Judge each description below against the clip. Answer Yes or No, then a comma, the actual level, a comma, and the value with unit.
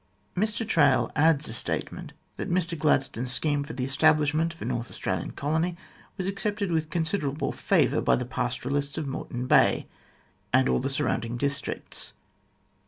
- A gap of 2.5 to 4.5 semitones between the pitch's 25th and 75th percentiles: Yes, average, 4.1 semitones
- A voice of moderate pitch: Yes, medium, 150 Hz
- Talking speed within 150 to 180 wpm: Yes, average, 155 wpm